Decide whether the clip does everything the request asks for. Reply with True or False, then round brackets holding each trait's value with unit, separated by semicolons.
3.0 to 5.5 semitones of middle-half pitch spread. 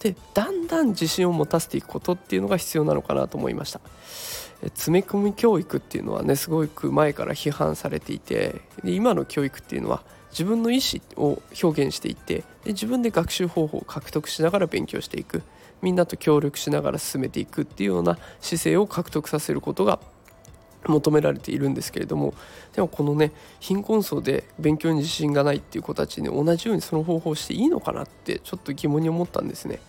True (5.1 semitones)